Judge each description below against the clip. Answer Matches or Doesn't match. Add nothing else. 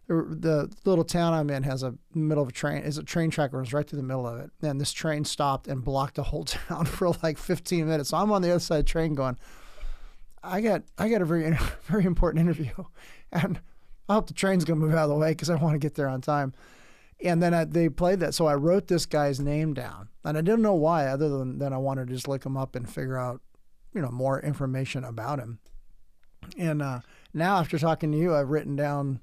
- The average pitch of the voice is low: Doesn't match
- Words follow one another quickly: Matches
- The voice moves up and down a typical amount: Matches